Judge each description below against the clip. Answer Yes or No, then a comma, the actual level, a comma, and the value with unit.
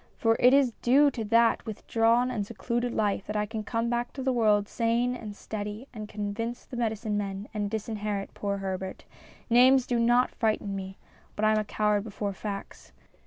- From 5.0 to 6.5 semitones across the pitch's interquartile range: No, narrow, 2.5 semitones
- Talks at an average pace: Yes, average, 195 wpm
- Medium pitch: No, high, 220 Hz